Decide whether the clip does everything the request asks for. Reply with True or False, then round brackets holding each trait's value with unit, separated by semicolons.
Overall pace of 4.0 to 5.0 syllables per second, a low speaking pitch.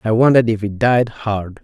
True (4.7 syllables/s; 110 Hz)